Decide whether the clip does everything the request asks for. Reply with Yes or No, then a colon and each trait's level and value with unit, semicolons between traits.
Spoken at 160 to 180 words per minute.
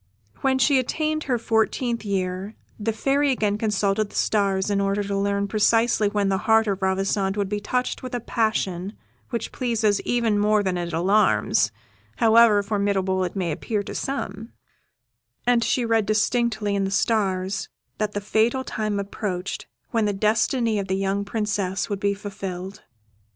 Yes: average, 165 wpm